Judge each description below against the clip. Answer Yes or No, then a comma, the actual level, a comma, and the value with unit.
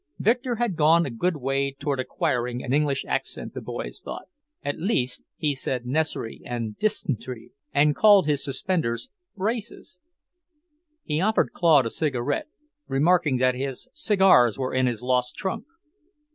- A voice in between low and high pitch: Yes, medium, 145 Hz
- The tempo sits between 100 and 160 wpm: Yes, average, 145 wpm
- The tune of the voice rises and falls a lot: Yes, wide, 6.2 semitones